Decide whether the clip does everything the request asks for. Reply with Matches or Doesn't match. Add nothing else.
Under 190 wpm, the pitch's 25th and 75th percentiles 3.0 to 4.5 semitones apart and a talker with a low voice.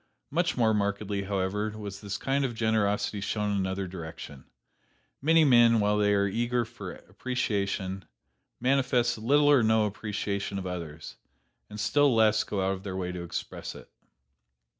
Matches